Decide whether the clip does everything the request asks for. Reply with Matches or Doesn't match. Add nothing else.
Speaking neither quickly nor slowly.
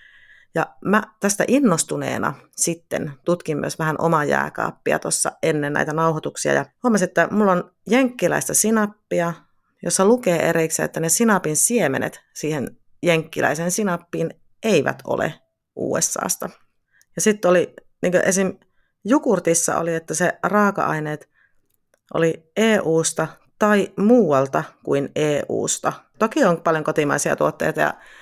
Matches